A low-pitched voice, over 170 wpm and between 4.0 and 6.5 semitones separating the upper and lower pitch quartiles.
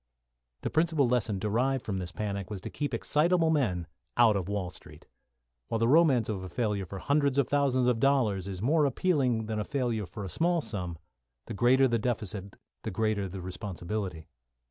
Yes: low, 110 Hz; average, 190 wpm; wide, 5.6 semitones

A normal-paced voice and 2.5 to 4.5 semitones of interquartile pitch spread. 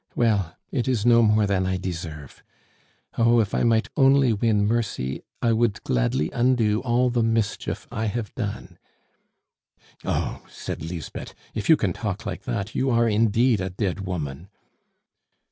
Yes: average, 155 wpm; average, 4.0 semitones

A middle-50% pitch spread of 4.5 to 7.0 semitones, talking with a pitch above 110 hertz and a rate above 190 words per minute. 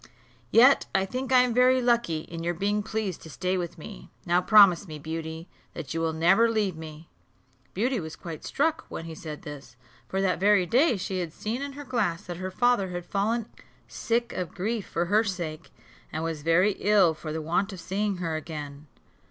Yes: average, 5.1 semitones; medium, 185 Hz; average, 200 wpm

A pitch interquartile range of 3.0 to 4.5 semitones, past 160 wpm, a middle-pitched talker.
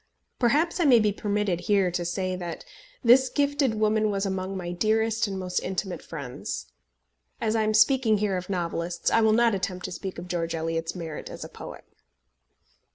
No: average, 3.8 semitones; average, 185 wpm; high, 195 Hz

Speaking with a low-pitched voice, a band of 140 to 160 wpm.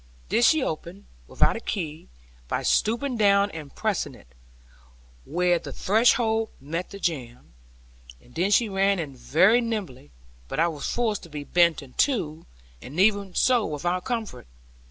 No: medium, 180 Hz; average, 155 wpm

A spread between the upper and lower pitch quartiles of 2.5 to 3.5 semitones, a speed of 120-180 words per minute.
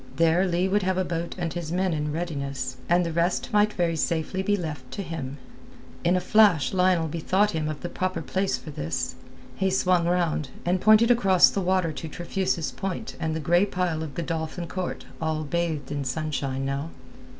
No: average, 3.0 semitones; average, 195 wpm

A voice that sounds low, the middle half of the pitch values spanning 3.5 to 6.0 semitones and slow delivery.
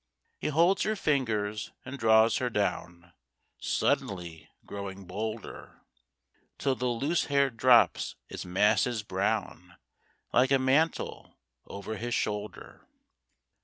Yes: low, 110 Hz; average, 4.7 semitones; slow, 110 wpm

